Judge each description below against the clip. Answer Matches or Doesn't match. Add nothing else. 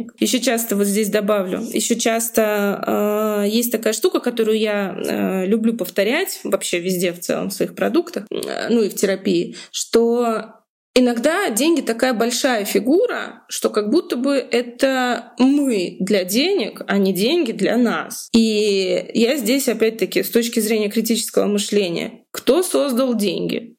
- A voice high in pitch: Matches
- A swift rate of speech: Doesn't match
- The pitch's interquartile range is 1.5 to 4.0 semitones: Matches